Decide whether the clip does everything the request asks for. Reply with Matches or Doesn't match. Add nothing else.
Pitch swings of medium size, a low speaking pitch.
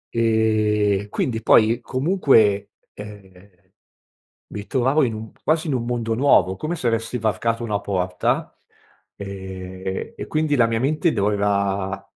Matches